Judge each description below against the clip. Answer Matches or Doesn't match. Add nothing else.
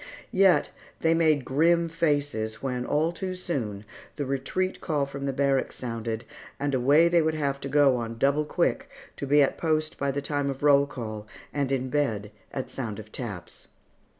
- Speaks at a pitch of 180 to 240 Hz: Doesn't match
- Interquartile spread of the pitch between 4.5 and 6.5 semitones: Doesn't match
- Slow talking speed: Doesn't match